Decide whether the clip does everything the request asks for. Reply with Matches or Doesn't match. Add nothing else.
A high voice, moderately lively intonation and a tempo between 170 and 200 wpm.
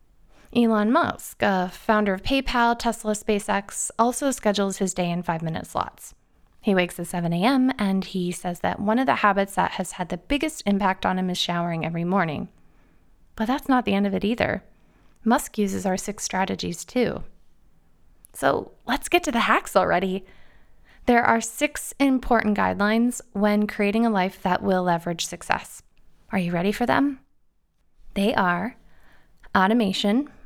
Doesn't match